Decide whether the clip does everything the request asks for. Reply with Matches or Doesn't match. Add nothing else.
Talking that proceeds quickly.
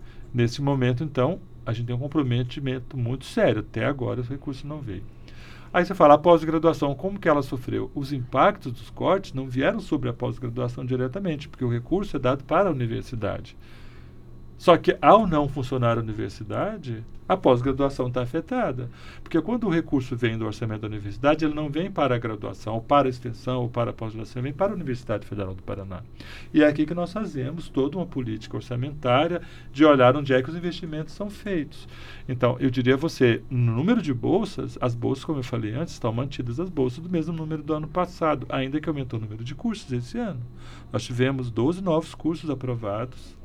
Matches